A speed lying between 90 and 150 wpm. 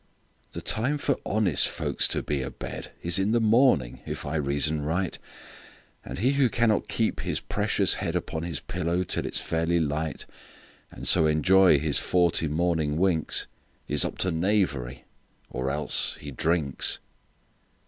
Yes: average, 140 wpm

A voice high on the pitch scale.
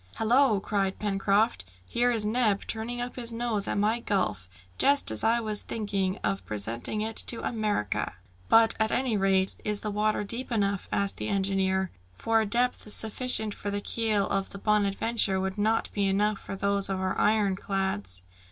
Yes: high, 205 Hz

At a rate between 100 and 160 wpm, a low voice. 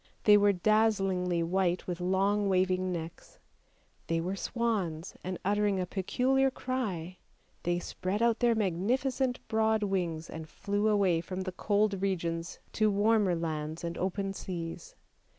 No: average, 140 wpm; high, 190 Hz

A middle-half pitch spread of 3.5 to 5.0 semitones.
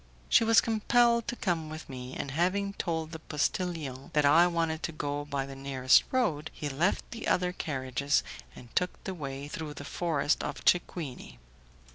Yes: average, 4.2 semitones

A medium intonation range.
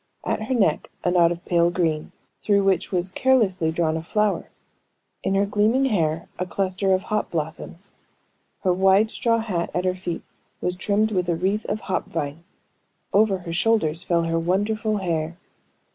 Yes: average, 3.6 semitones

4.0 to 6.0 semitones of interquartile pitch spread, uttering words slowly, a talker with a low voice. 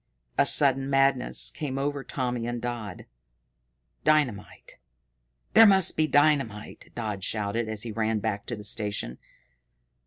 Yes: average, 4.5 semitones; slow, 130 wpm; low, 120 Hz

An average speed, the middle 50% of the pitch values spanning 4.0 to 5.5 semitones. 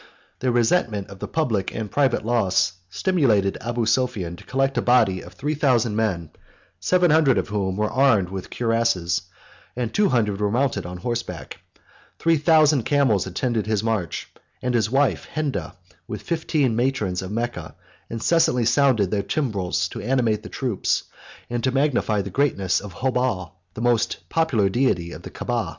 Yes: average, 165 wpm; average, 5.2 semitones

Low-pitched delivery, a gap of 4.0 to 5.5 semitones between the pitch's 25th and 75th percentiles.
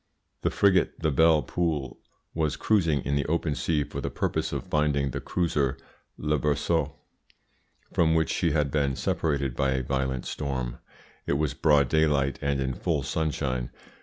No: very low, 75 Hz; narrow, 2.6 semitones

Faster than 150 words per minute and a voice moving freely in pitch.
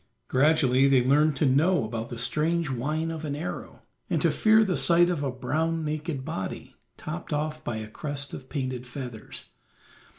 No: average, 175 wpm; average, 3.7 semitones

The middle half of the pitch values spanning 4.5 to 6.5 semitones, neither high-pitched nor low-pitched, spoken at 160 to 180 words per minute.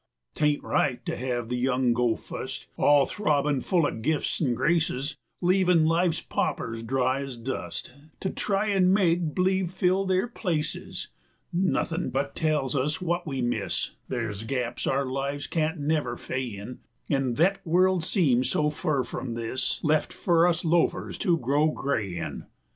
Yes: average, 5.2 semitones; medium, 150 Hz; average, 165 wpm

